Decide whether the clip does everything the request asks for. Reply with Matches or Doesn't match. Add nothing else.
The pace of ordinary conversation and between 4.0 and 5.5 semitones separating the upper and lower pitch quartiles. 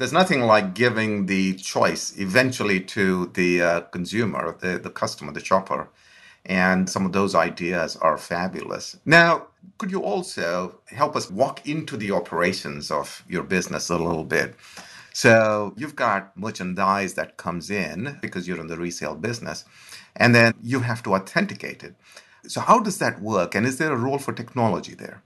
Matches